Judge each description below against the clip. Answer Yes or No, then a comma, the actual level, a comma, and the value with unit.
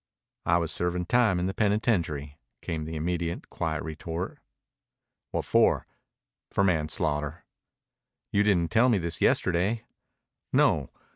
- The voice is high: No, very low, 85 Hz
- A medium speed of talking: No, slow, 125 wpm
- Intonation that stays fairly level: No, average, 3.6 semitones